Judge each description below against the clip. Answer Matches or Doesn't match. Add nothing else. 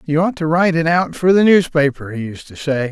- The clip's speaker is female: Doesn't match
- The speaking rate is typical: Doesn't match